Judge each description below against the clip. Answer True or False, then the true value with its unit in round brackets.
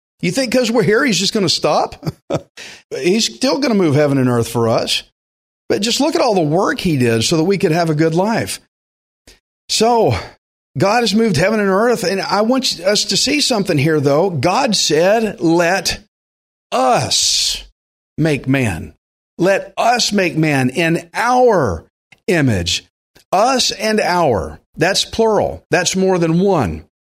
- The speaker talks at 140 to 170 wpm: True (165 wpm)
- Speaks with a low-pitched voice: False (180 Hz)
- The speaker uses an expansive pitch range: True (8.7 semitones)